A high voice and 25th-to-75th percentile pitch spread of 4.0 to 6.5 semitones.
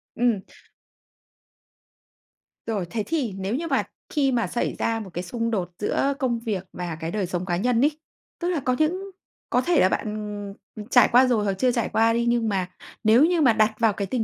Yes: high, 230 Hz; average, 4.3 semitones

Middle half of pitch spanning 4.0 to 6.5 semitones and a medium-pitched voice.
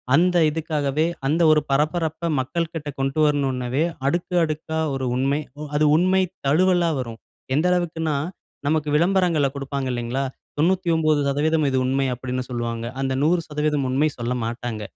No: average, 3.5 semitones; medium, 150 Hz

